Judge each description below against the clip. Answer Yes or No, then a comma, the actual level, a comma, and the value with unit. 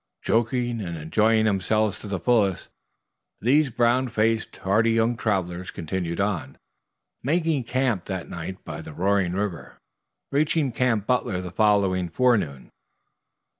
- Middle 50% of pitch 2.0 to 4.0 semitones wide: No, average, 4.6 semitones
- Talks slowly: Yes, slow, 130 wpm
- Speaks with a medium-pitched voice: No, low, 105 Hz